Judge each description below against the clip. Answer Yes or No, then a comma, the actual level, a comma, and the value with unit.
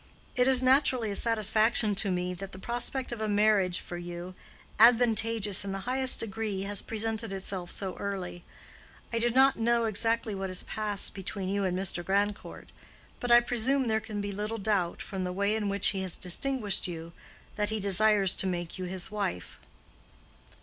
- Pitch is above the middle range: Yes, high, 205 Hz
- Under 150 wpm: No, average, 175 wpm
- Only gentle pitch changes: No, average, 3.1 semitones